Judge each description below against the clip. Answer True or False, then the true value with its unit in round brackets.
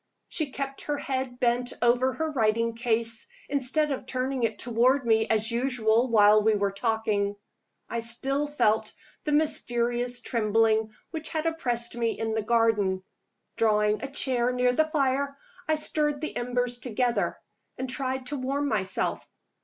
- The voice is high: True (245 Hz)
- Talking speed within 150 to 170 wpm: True (155 wpm)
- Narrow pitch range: False (3.3 semitones)